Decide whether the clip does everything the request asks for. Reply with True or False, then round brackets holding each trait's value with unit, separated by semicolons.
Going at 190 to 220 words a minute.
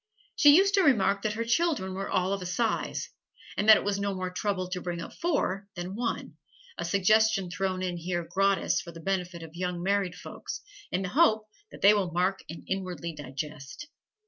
True (200 wpm)